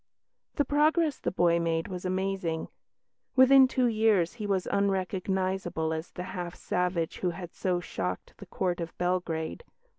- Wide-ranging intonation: No, average, 2.8 semitones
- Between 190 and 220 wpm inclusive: No, average, 150 wpm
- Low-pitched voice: No, medium, 185 Hz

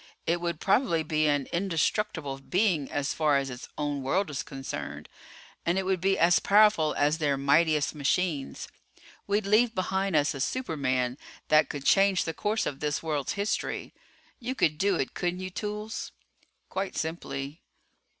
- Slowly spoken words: No, average, 160 wpm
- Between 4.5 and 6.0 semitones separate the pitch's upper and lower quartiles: Yes, average, 5.1 semitones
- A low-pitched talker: No, medium, 160 Hz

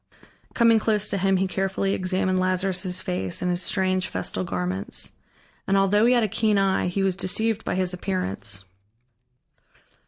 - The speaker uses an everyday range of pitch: No, narrow, 1.6 semitones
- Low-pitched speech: No, medium, 185 Hz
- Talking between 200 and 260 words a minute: No, average, 160 wpm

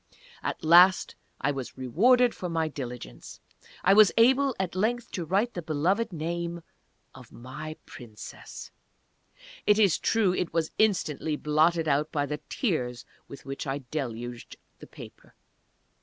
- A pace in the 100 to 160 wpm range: Yes, average, 140 wpm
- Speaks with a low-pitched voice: No, medium, 160 Hz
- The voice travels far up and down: Yes, wide, 5.8 semitones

